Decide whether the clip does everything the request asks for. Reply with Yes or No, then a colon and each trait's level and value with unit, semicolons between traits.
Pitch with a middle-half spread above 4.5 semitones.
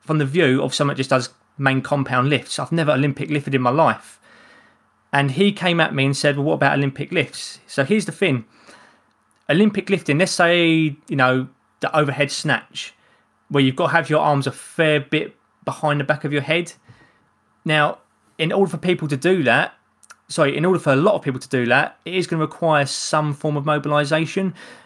No: average, 3.4 semitones